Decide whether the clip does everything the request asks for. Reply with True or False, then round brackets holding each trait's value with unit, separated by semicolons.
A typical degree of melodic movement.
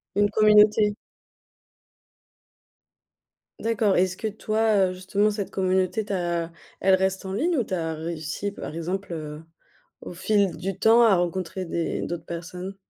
True (3.2 semitones)